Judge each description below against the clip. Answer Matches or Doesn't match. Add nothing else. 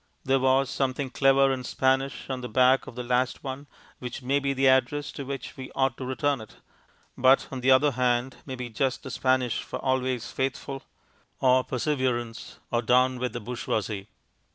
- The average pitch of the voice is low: Matches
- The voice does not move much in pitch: Matches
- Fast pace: Doesn't match